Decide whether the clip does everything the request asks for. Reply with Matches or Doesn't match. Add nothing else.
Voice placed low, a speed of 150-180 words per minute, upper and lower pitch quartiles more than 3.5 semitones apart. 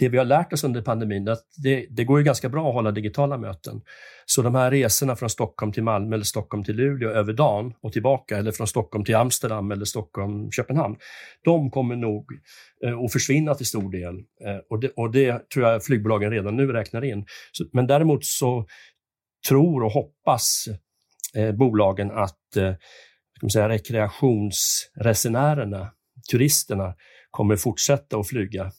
Matches